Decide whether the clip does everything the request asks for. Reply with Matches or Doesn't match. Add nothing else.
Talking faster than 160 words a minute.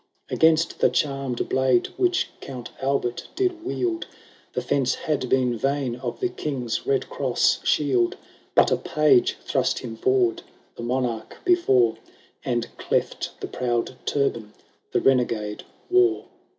Doesn't match